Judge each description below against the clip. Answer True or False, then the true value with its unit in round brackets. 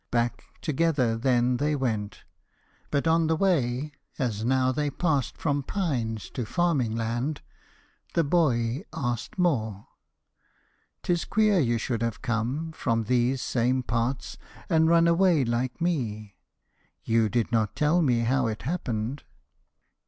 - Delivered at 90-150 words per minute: True (135 wpm)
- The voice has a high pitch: False (130 Hz)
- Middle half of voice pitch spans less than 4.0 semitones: False (5.3 semitones)